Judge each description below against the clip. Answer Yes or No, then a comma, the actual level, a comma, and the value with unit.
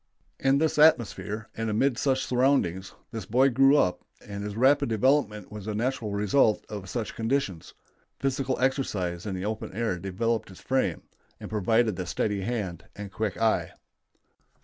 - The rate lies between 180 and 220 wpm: No, average, 160 wpm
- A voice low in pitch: Yes, low, 110 Hz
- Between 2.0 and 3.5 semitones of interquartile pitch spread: No, average, 4.5 semitones